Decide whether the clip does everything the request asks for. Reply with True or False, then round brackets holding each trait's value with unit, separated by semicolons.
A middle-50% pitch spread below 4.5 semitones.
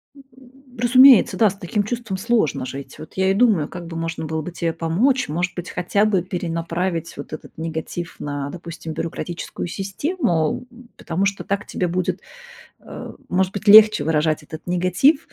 True (4.1 semitones)